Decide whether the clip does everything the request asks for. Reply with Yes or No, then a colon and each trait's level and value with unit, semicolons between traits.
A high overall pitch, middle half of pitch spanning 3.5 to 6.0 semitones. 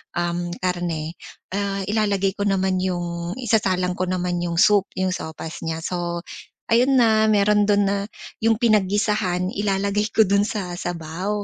No: high, 195 Hz; average, 2.8 semitones